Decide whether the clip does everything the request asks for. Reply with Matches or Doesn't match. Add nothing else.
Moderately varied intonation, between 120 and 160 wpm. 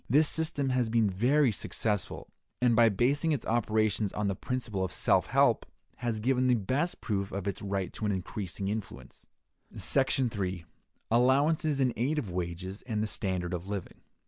Doesn't match